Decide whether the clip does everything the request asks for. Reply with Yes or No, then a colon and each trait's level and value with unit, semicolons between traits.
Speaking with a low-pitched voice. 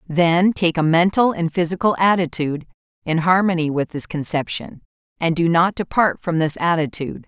No: medium, 170 Hz